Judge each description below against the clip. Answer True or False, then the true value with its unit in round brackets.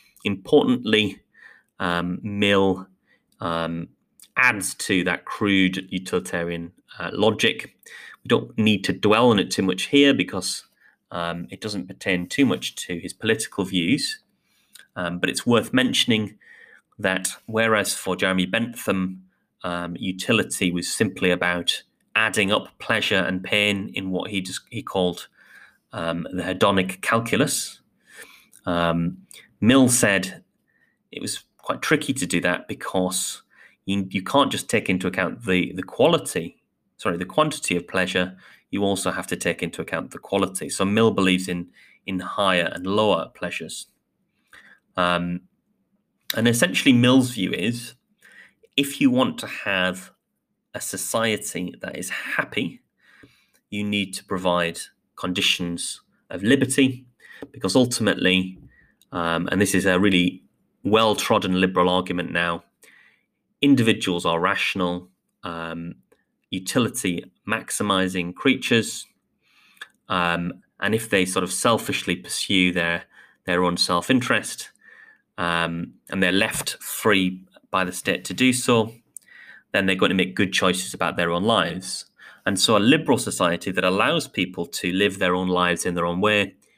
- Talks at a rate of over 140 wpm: False (135 wpm)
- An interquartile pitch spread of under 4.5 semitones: True (3.5 semitones)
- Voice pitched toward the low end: True (95 Hz)